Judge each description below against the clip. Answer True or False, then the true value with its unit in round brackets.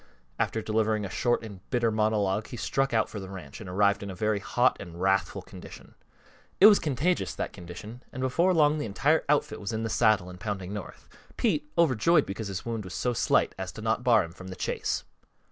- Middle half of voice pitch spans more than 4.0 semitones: True (4.5 semitones)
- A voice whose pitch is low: True (110 Hz)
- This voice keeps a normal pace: False (215 wpm)